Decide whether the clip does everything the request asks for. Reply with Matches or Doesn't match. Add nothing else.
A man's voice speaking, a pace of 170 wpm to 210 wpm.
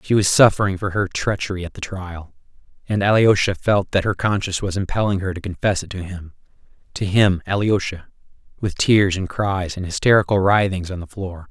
Matches